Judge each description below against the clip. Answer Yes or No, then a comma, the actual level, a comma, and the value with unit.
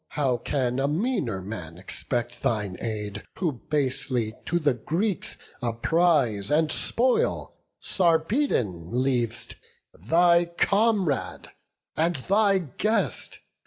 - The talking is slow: Yes, slow, 105 wpm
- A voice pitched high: No, medium, 140 Hz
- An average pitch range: No, wide, 7.1 semitones